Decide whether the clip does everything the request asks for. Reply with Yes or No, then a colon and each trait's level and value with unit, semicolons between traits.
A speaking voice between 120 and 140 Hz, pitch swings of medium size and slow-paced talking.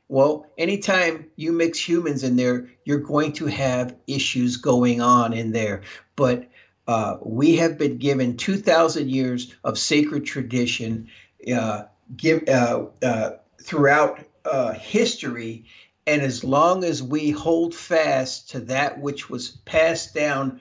Yes: low, 135 Hz; average, 4.2 semitones; slow, 130 wpm